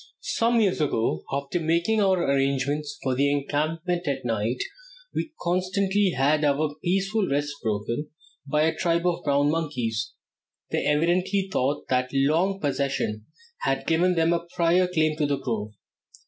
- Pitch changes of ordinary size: Yes, average, 4.4 semitones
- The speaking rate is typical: Yes, average, 150 wpm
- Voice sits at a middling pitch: Yes, medium, 155 Hz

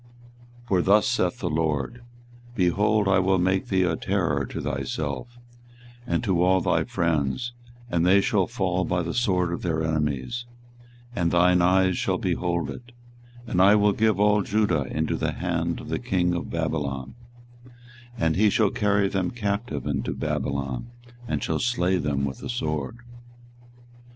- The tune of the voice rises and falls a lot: No, average, 4.1 semitones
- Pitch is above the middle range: No, very low, 90 Hz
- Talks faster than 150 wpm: Yes, average, 160 wpm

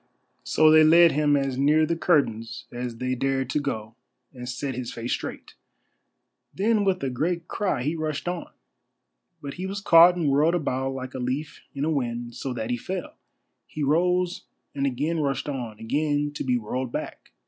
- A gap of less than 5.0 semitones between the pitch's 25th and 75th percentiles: Yes, average, 4.3 semitones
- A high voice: No, medium, 140 Hz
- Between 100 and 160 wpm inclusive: No, average, 185 wpm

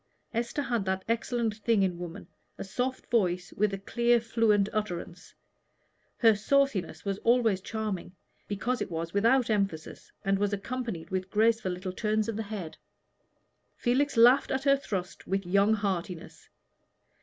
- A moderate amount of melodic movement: Yes, average, 3.6 semitones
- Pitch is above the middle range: Yes, high, 210 Hz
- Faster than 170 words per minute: No, average, 145 wpm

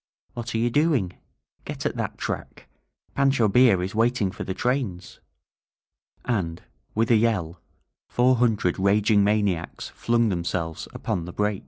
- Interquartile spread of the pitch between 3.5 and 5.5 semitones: Yes, average, 4.5 semitones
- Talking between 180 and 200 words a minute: No, average, 145 wpm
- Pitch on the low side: Yes, low, 105 Hz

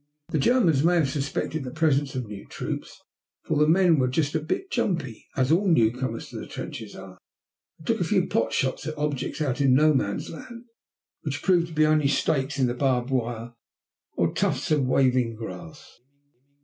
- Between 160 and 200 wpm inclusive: Yes, average, 190 wpm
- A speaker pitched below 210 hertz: Yes, medium, 140 Hz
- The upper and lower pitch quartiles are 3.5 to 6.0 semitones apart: Yes, average, 3.8 semitones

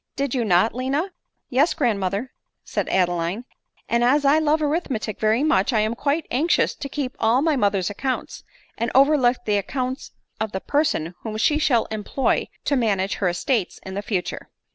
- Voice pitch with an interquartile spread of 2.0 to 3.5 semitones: No, wide, 5.5 semitones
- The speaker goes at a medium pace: Yes, average, 185 wpm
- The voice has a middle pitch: No, high, 240 Hz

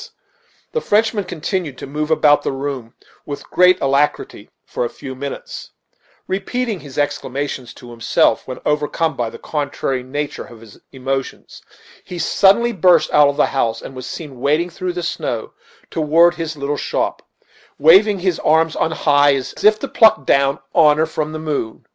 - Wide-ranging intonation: No, average, 4.1 semitones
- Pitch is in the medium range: Yes, medium, 150 Hz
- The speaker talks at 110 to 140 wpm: No, average, 165 wpm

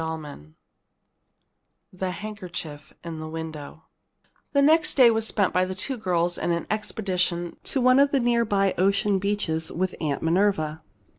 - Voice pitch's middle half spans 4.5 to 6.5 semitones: Yes, average, 4.8 semitones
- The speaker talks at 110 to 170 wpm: Yes, average, 160 wpm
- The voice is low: No, medium, 185 Hz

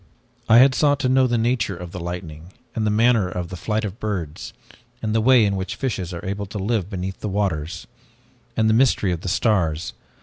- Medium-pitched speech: No, low, 100 Hz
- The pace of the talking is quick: Yes, fast, 215 wpm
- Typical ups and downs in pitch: Yes, average, 4.1 semitones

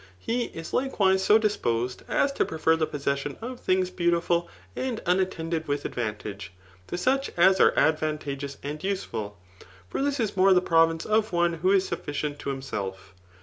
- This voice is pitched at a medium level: Yes, medium, 170 Hz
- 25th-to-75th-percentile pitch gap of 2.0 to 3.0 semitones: No, average, 5.2 semitones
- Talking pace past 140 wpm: Yes, average, 170 wpm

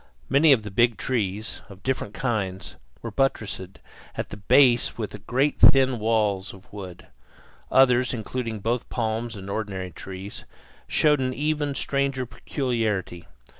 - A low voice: Yes, low, 115 Hz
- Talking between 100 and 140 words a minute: Yes, slow, 135 wpm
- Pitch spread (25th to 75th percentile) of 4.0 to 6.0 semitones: Yes, average, 4.6 semitones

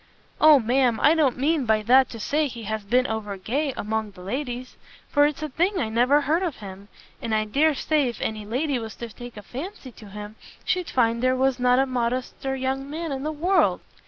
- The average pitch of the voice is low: No, very high, 255 Hz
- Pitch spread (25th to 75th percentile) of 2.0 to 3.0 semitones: No, average, 4.7 semitones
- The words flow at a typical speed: No, fast, 220 wpm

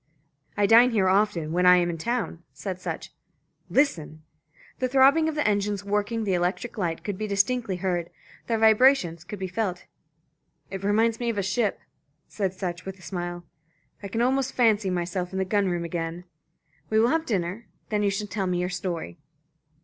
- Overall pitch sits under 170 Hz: No, high, 195 Hz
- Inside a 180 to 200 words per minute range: Yes, average, 190 wpm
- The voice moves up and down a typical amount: Yes, average, 3.9 semitones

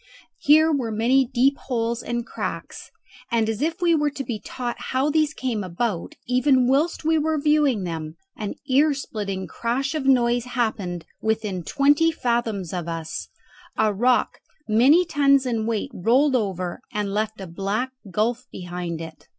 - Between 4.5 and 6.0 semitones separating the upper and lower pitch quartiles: Yes, average, 5.2 semitones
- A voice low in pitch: No, high, 240 Hz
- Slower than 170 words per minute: Yes, average, 160 wpm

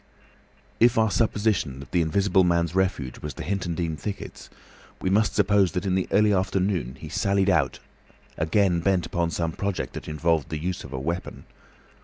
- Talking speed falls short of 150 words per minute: No, average, 180 wpm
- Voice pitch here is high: No, very low, 90 Hz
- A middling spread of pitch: Yes, average, 3.5 semitones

